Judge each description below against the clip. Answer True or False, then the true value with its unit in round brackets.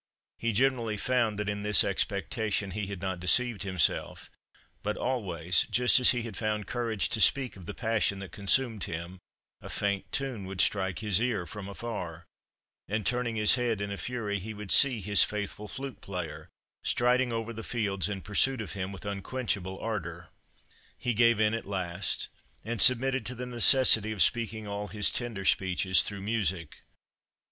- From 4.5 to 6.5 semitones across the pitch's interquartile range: False (3.3 semitones)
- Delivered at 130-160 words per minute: False (175 wpm)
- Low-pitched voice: True (105 Hz)